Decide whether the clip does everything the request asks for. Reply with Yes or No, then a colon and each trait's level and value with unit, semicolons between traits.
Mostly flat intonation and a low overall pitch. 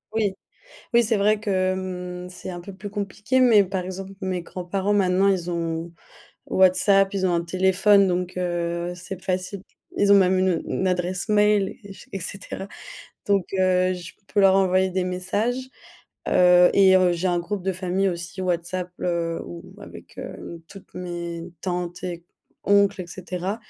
No: narrow, 1.7 semitones; medium, 185 Hz